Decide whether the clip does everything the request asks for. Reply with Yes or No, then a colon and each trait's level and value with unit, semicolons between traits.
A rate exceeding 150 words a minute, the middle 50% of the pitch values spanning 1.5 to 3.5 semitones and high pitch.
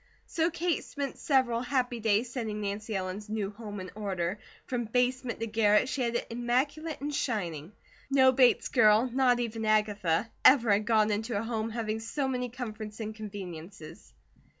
Yes: average, 170 wpm; average, 3.1 semitones; high, 225 Hz